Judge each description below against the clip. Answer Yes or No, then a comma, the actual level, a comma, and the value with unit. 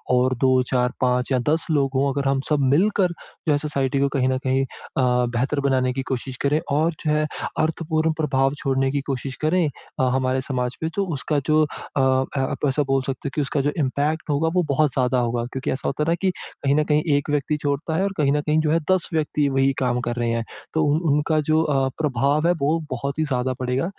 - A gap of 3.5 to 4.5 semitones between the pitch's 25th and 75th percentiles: No, average, 2.7 semitones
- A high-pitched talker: No, medium, 140 Hz